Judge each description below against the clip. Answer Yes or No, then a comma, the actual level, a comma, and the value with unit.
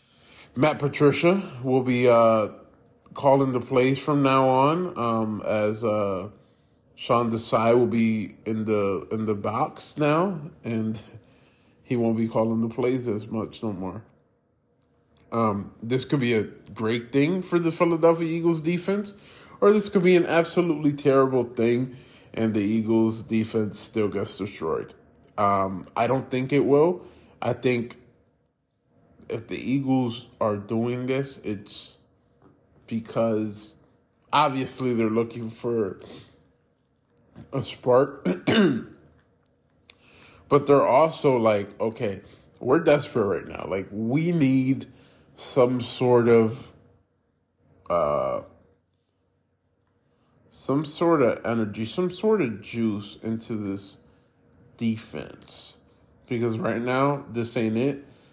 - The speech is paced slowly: Yes, slow, 120 wpm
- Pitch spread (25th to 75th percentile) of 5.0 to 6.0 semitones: No, average, 3.6 semitones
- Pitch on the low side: Yes, low, 120 Hz